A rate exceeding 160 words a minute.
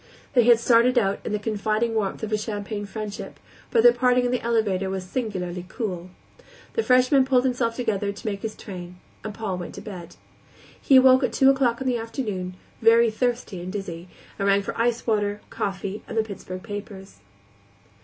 Yes: average, 185 wpm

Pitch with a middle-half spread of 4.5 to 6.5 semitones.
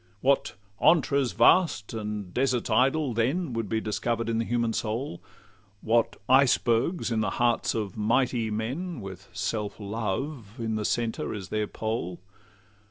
No: average, 3.2 semitones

